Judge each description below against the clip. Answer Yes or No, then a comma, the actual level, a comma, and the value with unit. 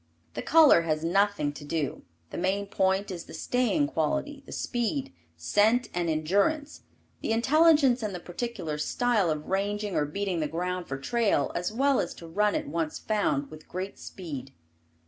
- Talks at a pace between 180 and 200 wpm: No, average, 170 wpm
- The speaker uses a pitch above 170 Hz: Yes, high, 190 Hz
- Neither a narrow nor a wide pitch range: No, wide, 6.4 semitones